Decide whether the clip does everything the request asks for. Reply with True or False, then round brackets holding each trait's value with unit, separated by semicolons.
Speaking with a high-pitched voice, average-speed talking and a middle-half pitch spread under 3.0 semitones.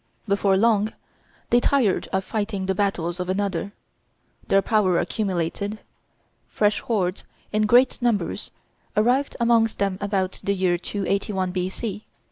False (200 Hz; 125 wpm; 2.5 semitones)